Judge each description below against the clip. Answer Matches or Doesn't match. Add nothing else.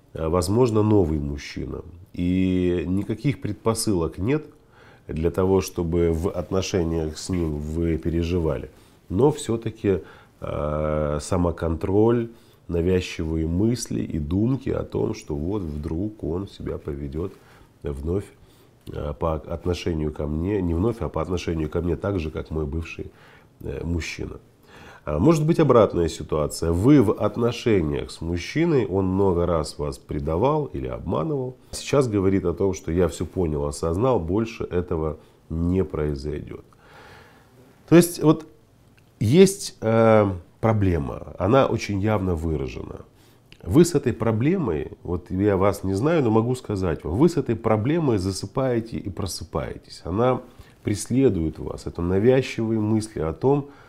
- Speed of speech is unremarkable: Matches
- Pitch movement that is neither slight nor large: Doesn't match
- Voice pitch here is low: Matches